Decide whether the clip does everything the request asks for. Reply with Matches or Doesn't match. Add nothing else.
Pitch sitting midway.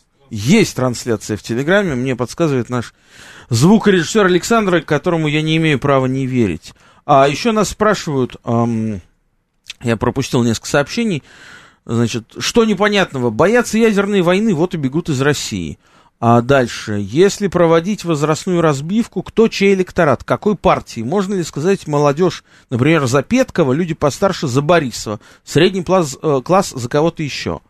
Matches